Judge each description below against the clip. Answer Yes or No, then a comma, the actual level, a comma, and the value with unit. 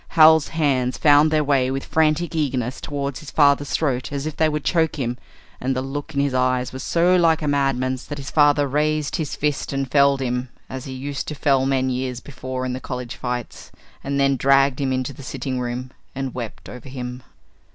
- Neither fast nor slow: No, fast, 210 wpm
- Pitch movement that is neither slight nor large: No, narrow, 2.3 semitones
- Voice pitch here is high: No, low, 135 Hz